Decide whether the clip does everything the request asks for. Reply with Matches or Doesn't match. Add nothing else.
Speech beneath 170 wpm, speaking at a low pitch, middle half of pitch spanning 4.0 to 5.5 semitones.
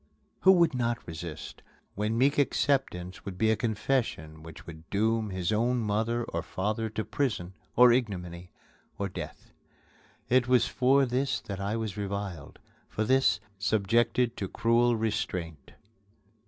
Matches